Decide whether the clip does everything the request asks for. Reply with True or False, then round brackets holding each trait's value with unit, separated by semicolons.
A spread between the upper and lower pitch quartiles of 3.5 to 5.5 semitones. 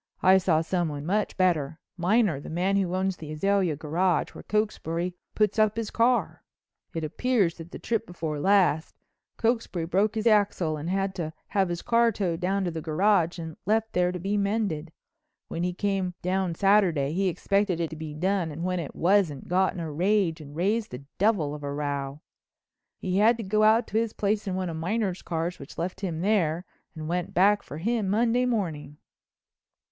True (4.1 semitones)